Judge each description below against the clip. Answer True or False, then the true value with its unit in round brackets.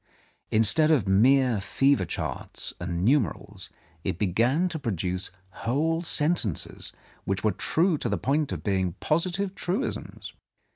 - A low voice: True (130 Hz)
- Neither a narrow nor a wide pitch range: False (8.4 semitones)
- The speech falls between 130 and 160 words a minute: True (135 wpm)